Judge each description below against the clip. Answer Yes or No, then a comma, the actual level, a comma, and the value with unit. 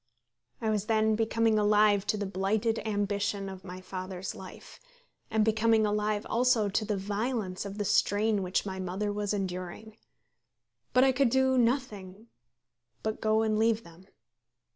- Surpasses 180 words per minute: No, average, 155 wpm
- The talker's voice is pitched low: No, high, 210 Hz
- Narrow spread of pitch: Yes, narrow, 2.2 semitones